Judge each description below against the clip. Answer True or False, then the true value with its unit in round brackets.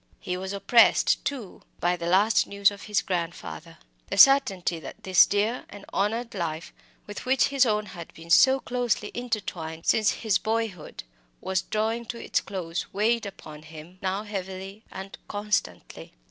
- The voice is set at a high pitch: True (200 Hz)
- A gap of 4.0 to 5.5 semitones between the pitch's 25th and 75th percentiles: False (3.6 semitones)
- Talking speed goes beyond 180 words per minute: False (160 wpm)